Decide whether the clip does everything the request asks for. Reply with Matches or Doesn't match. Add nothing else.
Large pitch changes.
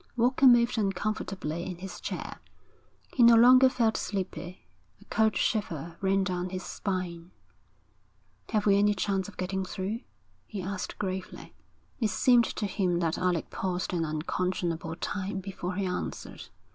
Doesn't match